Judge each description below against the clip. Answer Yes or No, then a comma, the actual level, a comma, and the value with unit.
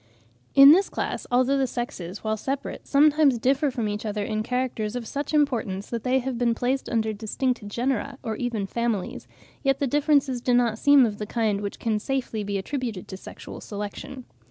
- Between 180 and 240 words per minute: Yes, average, 190 wpm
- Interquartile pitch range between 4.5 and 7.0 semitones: No, average, 4.0 semitones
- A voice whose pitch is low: No, high, 240 Hz